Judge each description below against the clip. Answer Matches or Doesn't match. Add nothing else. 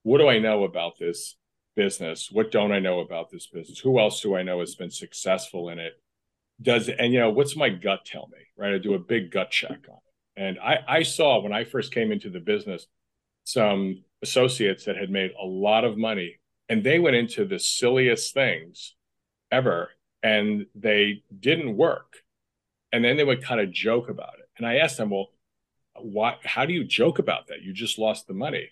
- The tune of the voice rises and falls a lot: Doesn't match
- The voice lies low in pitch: Matches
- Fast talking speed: Matches